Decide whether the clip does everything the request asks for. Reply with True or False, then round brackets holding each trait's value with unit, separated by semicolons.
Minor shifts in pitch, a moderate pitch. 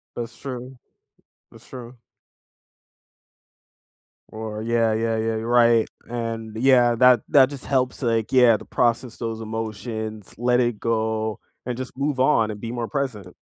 False (2.0 semitones; 115 Hz)